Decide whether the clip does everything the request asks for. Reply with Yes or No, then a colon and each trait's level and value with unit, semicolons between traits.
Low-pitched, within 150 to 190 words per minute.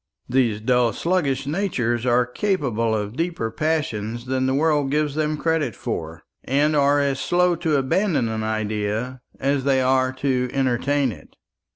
Yes: low, 130 Hz; average, 155 wpm